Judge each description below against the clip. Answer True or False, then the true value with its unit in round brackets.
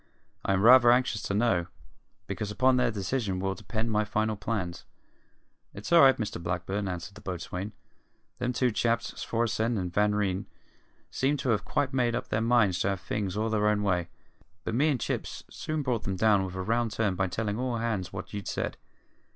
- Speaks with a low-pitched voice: True (105 Hz)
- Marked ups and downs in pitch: False (3.4 semitones)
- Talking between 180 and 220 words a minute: True (200 wpm)